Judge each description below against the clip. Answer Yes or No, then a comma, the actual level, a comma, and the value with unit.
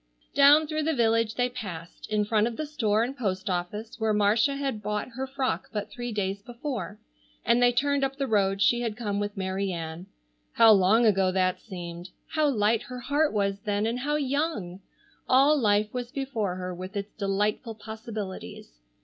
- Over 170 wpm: Yes, average, 185 wpm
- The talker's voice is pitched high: Yes, high, 220 Hz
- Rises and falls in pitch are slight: No, average, 4.3 semitones